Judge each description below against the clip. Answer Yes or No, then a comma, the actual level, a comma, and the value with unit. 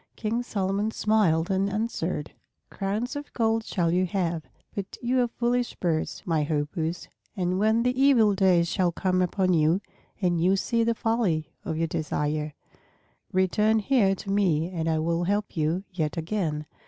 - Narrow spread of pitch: No, average, 4.7 semitones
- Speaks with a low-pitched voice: No, medium, 185 Hz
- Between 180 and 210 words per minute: No, average, 165 wpm